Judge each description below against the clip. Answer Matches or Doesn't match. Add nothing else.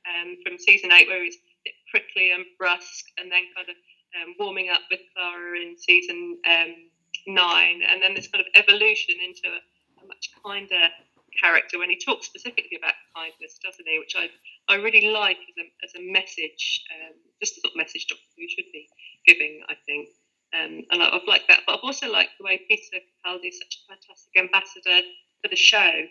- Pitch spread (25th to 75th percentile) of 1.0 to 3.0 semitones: Doesn't match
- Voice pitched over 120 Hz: Matches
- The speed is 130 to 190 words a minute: Doesn't match